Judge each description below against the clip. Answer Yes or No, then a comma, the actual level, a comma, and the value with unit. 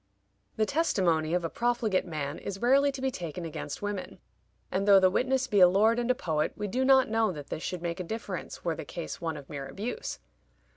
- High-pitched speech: Yes, high, 195 Hz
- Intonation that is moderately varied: No, wide, 6.2 semitones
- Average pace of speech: No, fast, 225 wpm